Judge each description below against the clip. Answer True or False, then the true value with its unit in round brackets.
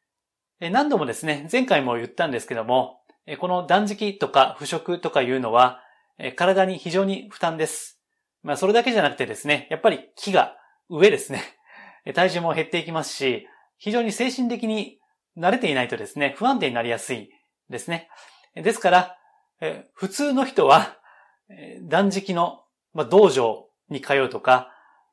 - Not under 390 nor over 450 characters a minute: False (295 characters per minute)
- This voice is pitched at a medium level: True (175 Hz)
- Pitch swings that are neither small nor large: False (6.9 semitones)